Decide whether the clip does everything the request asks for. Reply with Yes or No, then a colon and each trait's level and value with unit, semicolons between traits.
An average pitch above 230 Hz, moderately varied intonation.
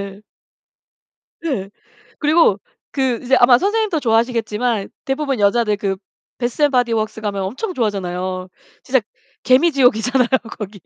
Yes: high, 240 Hz; average, 4.6 semitones